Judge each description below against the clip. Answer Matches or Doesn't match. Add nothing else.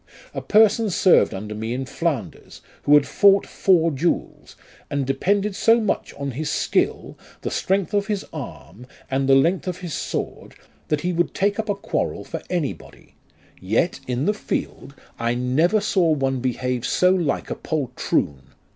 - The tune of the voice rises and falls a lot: Matches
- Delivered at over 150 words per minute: Matches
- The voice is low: Doesn't match